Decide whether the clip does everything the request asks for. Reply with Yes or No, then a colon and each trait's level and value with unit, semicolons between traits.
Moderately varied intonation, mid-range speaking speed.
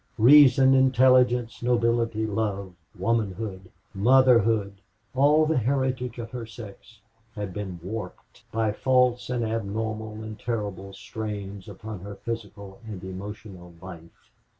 No: average, 3.5 semitones; slow, 115 wpm